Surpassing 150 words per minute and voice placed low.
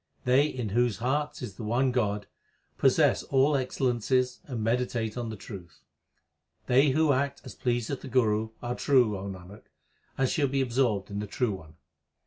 Yes: average, 170 wpm; low, 120 Hz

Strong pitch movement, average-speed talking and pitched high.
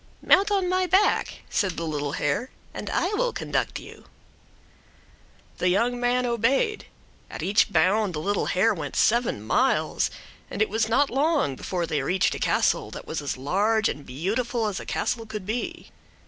Yes: wide, 5.8 semitones; average, 175 wpm; high, 215 Hz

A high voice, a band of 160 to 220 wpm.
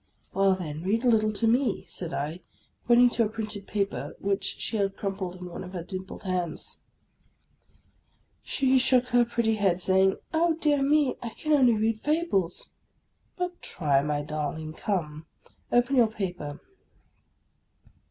Yes: high, 205 Hz; average, 165 wpm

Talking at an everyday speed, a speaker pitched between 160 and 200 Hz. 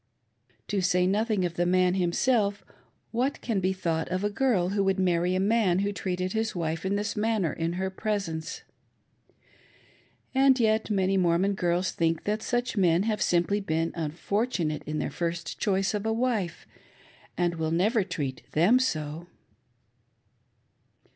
Yes: average, 155 wpm; high, 190 Hz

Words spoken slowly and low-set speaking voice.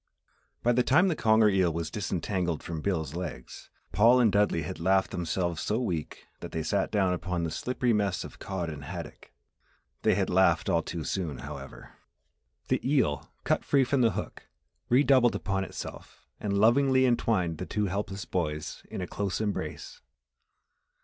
No: average, 170 wpm; very low, 95 Hz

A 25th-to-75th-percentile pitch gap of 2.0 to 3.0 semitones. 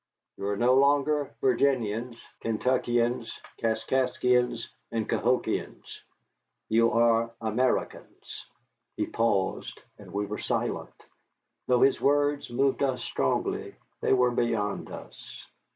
Yes: narrow, 2.4 semitones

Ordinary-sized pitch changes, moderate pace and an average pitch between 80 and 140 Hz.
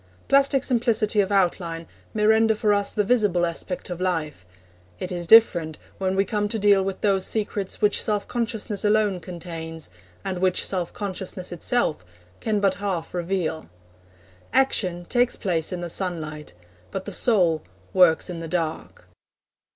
No: average, 3.4 semitones; average, 155 wpm; high, 190 Hz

